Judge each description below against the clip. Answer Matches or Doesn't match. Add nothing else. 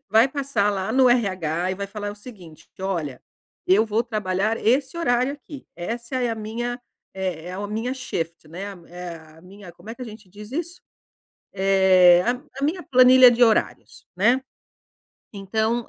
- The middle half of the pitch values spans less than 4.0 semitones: Doesn't match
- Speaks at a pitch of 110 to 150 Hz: Doesn't match